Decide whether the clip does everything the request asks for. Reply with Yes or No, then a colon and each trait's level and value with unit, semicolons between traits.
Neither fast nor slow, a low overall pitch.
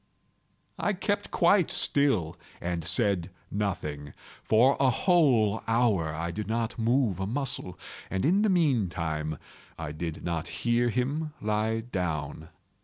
No: slow, 130 wpm; low, 110 Hz